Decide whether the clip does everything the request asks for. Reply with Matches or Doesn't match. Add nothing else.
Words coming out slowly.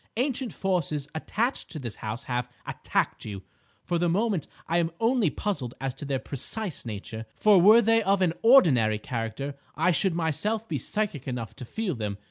Doesn't match